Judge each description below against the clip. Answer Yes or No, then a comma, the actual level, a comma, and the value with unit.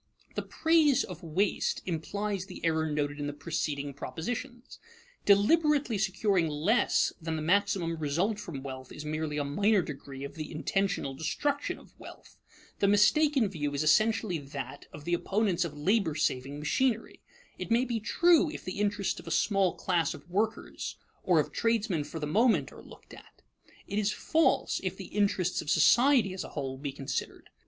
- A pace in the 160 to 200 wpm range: Yes, average, 175 wpm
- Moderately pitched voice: Yes, medium, 180 Hz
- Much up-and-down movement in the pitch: Yes, wide, 6.1 semitones